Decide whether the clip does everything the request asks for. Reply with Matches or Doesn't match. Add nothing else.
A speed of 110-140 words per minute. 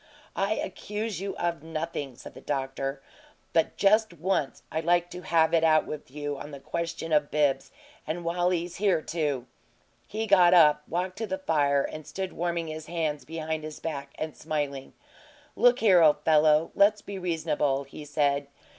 Doesn't match